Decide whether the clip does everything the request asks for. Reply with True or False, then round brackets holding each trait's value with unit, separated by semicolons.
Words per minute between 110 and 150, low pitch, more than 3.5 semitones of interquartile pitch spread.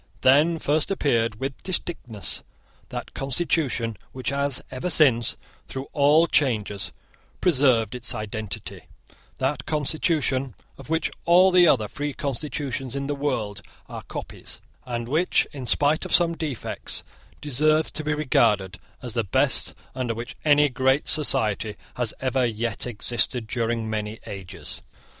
True (135 wpm; 130 Hz; 4.4 semitones)